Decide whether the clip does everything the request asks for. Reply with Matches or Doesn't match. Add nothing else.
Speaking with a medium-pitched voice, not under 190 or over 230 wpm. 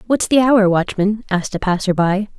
Doesn't match